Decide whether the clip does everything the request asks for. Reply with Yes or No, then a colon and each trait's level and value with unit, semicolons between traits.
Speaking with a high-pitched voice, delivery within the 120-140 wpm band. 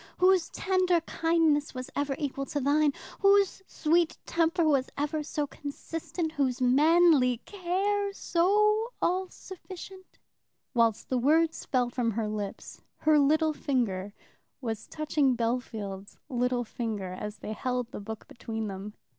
Yes: very high, 285 Hz; slow, 135 wpm